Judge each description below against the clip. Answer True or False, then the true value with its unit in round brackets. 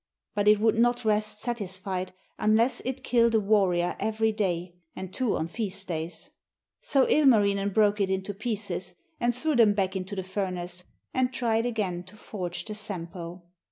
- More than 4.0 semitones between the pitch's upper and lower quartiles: False (3.4 semitones)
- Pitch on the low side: False (205 Hz)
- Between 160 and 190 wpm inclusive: True (165 wpm)